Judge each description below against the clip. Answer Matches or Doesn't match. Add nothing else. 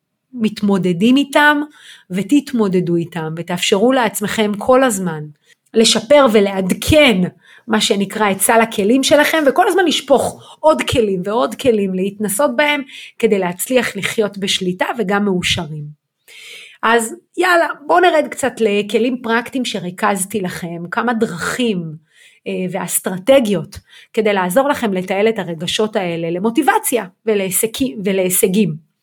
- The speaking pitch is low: Doesn't match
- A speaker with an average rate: Matches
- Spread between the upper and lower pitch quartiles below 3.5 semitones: Doesn't match